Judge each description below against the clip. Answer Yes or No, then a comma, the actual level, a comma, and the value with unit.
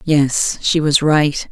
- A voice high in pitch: No, medium, 150 Hz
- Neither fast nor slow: Yes, average, 160 wpm